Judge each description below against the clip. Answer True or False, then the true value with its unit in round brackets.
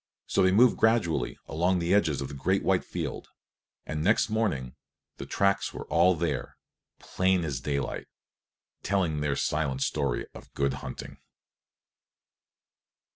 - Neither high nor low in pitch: False (85 Hz)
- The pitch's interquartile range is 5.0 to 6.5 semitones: True (5.4 semitones)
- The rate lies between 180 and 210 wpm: False (135 wpm)